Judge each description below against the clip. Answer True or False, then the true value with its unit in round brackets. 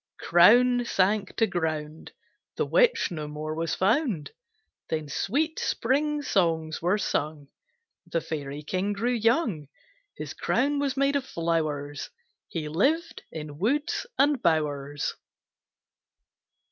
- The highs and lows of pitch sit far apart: True (8.7 semitones)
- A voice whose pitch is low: False (185 Hz)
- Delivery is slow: True (120 wpm)